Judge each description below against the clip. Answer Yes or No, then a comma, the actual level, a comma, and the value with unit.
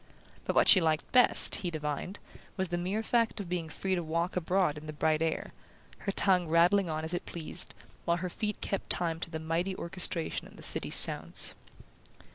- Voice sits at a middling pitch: Yes, medium, 175 Hz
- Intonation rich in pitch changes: No, average, 2.8 semitones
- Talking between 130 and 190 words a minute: No, average, 200 wpm